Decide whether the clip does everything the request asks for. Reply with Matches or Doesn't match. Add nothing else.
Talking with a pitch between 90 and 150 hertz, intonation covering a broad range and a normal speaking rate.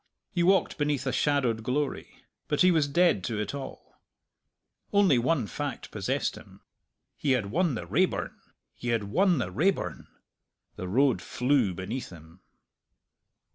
Matches